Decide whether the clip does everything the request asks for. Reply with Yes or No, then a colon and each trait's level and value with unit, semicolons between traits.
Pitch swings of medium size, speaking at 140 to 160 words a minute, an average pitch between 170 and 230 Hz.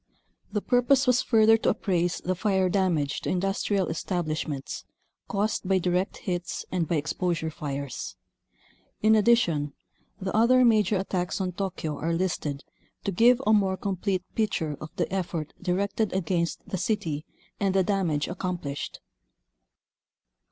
Yes: average, 3.5 semitones; average, 145 wpm; medium, 185 Hz